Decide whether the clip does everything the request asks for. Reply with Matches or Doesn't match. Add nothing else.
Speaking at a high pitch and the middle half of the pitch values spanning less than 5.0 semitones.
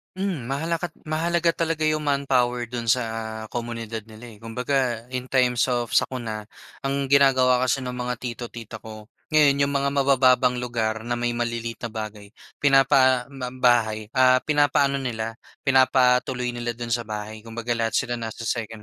Doesn't match